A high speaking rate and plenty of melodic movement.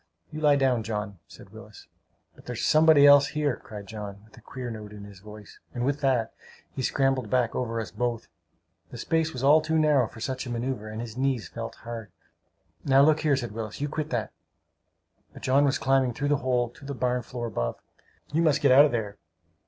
No: fast, 215 wpm; average, 4.1 semitones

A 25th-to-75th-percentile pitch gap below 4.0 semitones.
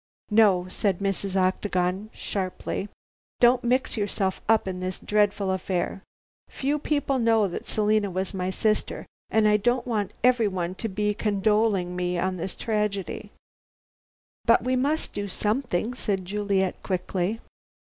Yes: average, 2.9 semitones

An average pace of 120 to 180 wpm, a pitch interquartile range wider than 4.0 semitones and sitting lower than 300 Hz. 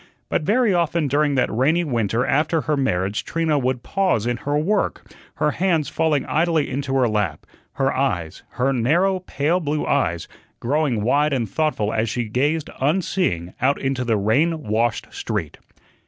Yes: average, 165 wpm; average, 5.1 semitones; medium, 140 Hz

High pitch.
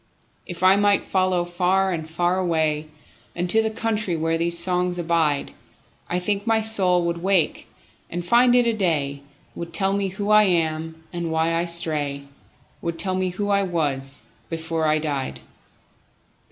No: medium, 175 Hz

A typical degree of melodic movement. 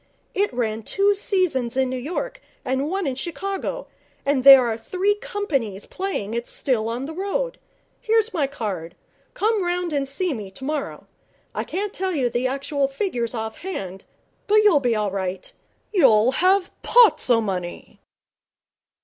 No: wide, 8.6 semitones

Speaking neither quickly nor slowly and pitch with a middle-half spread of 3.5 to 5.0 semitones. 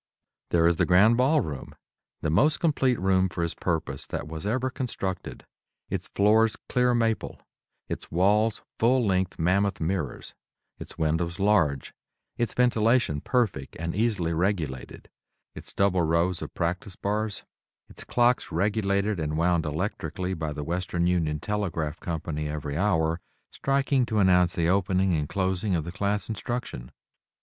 Yes: average, 145 wpm; average, 4.6 semitones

